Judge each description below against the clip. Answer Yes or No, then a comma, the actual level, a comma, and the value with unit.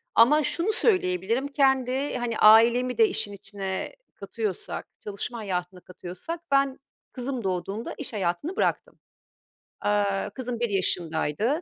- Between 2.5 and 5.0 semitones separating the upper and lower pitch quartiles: No, wide, 5.6 semitones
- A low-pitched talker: No, high, 225 Hz